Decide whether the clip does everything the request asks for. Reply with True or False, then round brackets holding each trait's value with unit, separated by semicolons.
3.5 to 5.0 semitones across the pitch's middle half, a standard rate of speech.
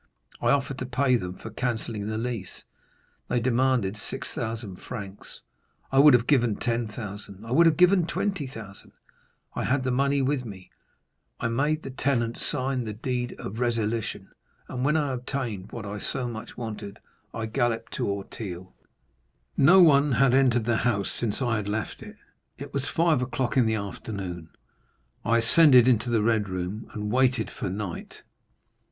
True (3.8 semitones; 165 wpm)